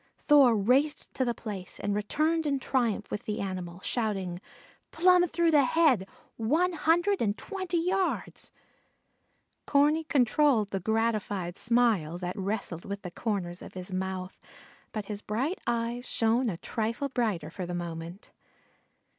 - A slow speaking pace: No, average, 145 wpm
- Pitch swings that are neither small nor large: No, wide, 7.1 semitones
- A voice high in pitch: Yes, high, 225 Hz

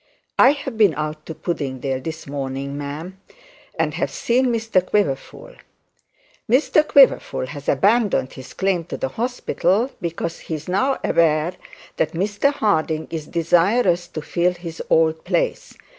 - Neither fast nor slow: Yes, average, 145 wpm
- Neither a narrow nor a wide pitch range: No, wide, 6.3 semitones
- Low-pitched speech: No, medium, 170 Hz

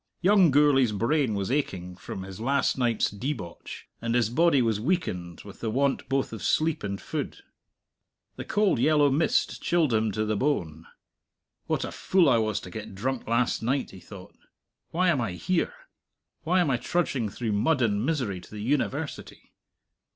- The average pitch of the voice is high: No, low, 120 Hz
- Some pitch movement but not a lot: No, wide, 6.0 semitones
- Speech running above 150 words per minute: Yes, average, 175 wpm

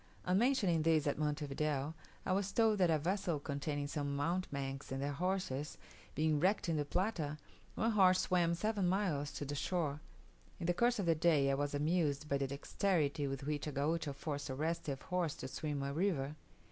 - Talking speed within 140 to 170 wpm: No, average, 195 wpm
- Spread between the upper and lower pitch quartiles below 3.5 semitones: No, average, 4.1 semitones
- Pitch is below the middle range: No, medium, 155 Hz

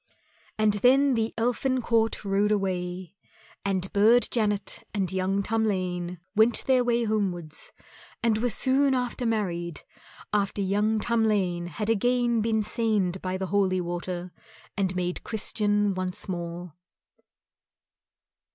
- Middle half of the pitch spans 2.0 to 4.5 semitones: Yes, average, 3.5 semitones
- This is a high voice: Yes, high, 205 Hz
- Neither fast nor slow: No, slow, 125 wpm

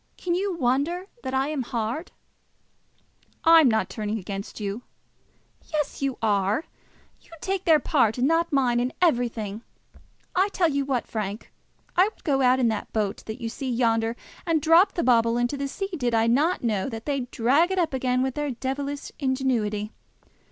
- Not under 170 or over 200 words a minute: Yes, average, 180 wpm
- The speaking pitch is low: No, very high, 260 Hz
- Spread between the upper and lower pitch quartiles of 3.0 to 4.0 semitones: No, average, 5.1 semitones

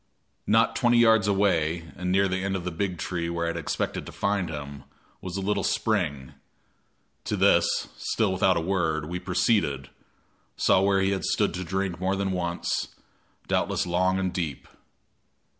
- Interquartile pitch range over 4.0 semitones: No, narrow, 2.6 semitones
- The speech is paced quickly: No, average, 175 wpm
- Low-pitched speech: Yes, very low, 95 Hz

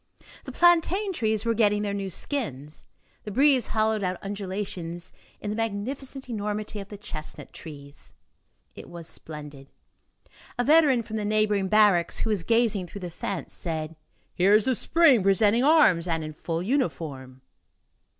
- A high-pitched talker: Yes, high, 205 Hz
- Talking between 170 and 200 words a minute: No, average, 155 wpm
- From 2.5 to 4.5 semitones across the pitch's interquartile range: No, average, 5.1 semitones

